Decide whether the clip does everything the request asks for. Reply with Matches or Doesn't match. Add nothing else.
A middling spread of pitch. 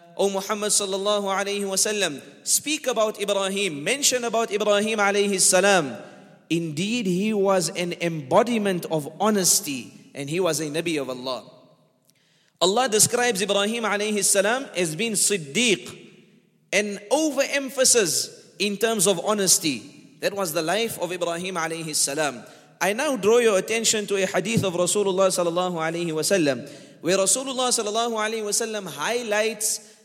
Matches